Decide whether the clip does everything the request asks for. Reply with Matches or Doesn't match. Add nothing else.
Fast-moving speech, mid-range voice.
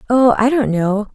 Doesn't match